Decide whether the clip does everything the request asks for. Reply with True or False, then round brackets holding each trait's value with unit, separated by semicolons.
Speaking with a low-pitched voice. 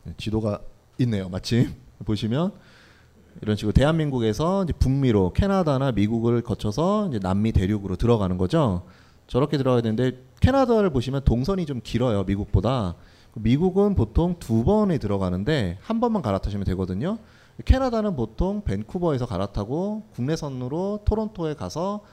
True (125 Hz)